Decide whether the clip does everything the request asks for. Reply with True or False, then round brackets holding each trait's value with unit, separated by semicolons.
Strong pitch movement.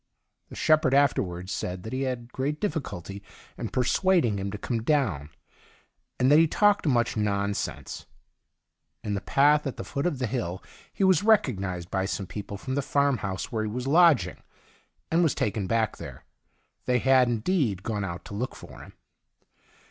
True (6.0 semitones)